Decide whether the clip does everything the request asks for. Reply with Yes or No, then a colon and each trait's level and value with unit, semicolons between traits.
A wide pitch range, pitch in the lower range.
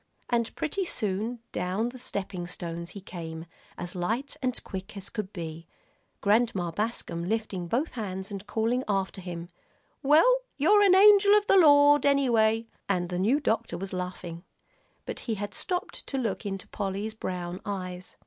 No: wide, 5.7 semitones; high, 205 Hz